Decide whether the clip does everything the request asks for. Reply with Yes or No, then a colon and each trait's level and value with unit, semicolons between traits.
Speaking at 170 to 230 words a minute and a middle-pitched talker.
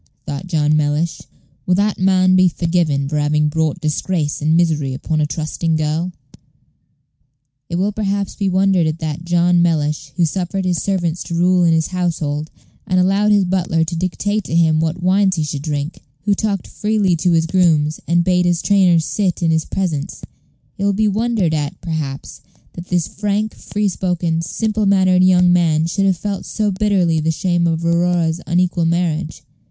Yes: average, 180 wpm; medium, 175 Hz